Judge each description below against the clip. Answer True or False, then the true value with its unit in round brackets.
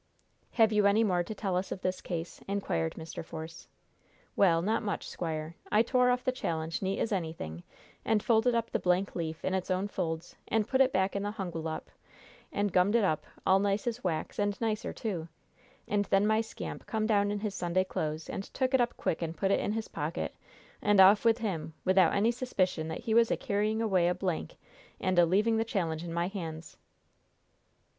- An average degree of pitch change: True (4.2 semitones)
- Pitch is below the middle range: False (195 Hz)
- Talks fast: True (210 wpm)